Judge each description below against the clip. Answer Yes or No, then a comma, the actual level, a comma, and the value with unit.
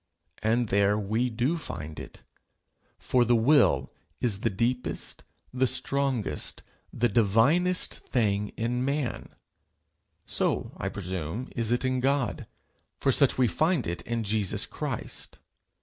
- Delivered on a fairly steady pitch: No, average, 3.7 semitones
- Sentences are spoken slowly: Yes, slow, 130 wpm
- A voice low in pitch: Yes, low, 120 Hz